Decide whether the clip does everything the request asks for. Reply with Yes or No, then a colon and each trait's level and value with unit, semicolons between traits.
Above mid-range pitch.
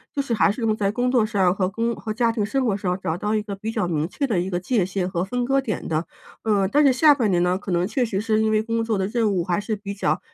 Yes: high, 210 Hz